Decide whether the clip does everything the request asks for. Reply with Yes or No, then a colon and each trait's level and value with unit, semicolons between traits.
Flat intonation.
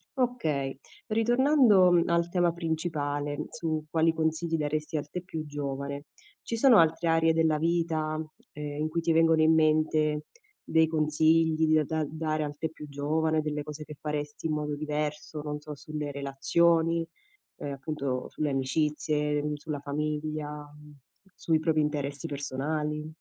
Yes: narrow, 1.6 semitones